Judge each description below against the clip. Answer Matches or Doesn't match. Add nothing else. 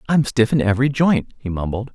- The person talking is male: Matches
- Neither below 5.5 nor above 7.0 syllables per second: Matches